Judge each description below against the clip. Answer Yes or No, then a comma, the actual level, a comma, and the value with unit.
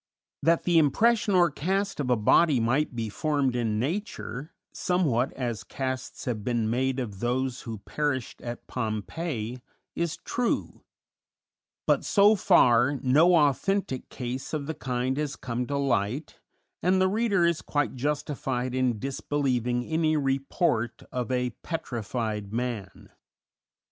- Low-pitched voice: Yes, low, 130 Hz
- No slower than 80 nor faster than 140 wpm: Yes, slow, 135 wpm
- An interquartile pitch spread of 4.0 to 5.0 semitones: Yes, average, 4.6 semitones